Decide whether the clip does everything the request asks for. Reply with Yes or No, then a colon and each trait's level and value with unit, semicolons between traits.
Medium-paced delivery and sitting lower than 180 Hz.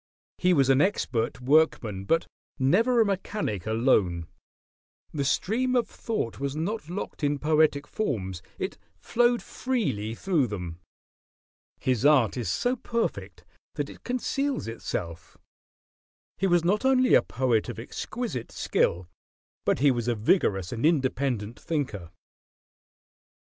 No: slow, 130 wpm; medium, 140 Hz